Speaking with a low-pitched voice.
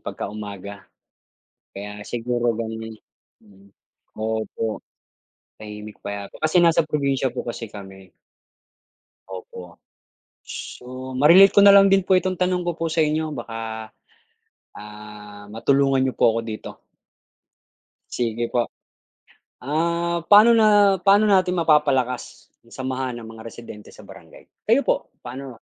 Yes: low, 125 Hz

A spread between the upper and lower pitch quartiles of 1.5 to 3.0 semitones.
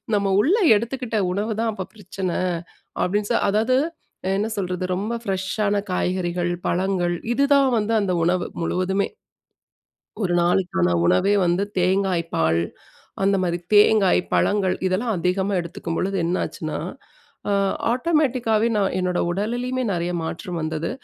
No: average, 3.4 semitones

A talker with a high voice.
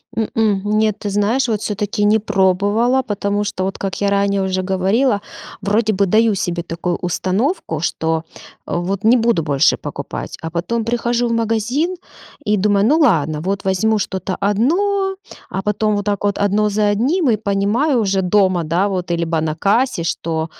Yes: high, 205 Hz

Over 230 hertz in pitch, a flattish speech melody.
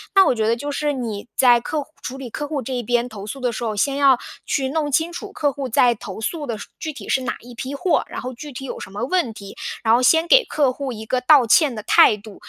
No: very high, 255 Hz; average, 4.0 semitones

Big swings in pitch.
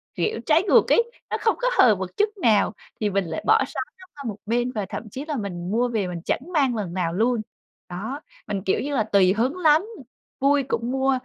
Yes: wide, 6.1 semitones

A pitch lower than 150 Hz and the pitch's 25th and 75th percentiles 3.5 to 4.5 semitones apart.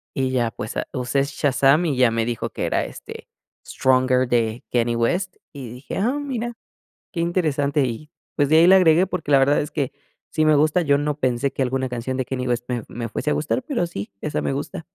Yes: medium, 140 Hz; average, 3.8 semitones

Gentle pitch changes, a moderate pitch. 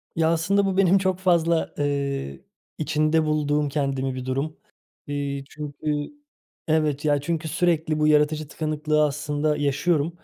Yes: narrow, 1.9 semitones; medium, 150 Hz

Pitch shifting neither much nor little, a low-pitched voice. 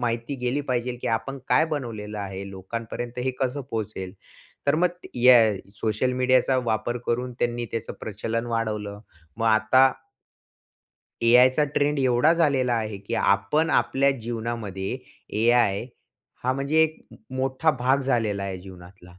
Yes: average, 3.3 semitones; low, 120 Hz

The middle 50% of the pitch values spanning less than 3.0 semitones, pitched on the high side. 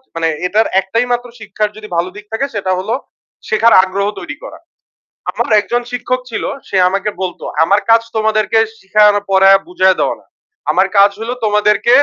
Yes: narrow, 2.6 semitones; high, 210 Hz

